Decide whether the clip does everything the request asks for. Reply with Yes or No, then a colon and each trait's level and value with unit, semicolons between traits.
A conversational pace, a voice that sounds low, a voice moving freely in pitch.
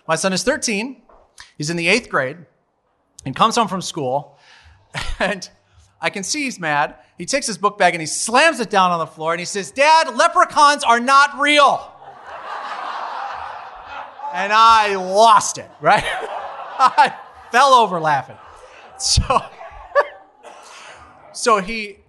No: average, 145 wpm; high, 220 Hz; wide, 8.0 semitones